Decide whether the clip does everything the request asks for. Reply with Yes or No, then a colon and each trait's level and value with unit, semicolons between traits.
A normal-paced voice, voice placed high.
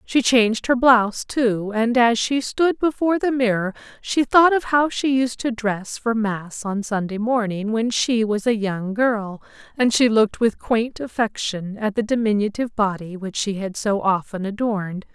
Yes: average, 185 wpm; high, 225 Hz